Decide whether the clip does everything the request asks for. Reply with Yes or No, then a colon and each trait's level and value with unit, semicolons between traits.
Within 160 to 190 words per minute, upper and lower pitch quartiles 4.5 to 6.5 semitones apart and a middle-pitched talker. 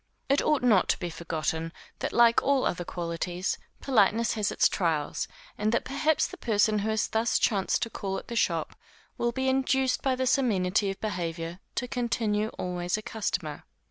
No: average, 185 wpm; average, 5.3 semitones; high, 215 Hz